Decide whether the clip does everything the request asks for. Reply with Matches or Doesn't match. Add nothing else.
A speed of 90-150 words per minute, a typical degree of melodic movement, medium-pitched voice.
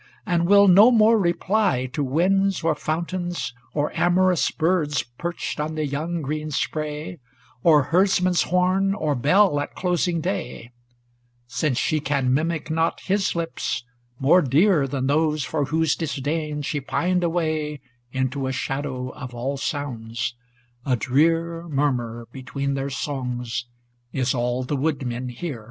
Matches